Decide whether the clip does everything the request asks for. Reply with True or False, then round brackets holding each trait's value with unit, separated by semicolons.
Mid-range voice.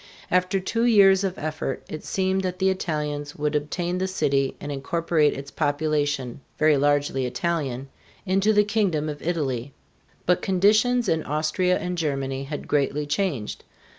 True (155 Hz)